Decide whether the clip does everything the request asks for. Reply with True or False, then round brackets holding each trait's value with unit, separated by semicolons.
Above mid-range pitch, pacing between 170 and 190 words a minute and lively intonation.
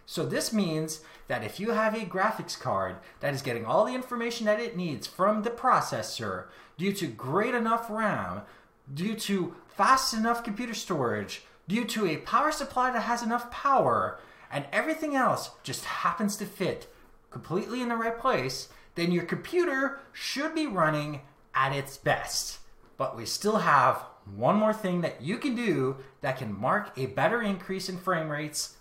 True (200 Hz; 175 wpm; 7.2 semitones)